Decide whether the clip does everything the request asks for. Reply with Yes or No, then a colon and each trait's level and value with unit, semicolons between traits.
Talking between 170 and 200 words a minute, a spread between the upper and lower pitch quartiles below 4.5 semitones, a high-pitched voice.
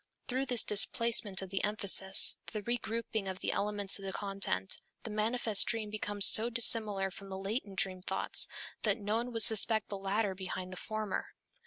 Yes: average, 180 wpm; narrow, 2.5 semitones; high, 210 Hz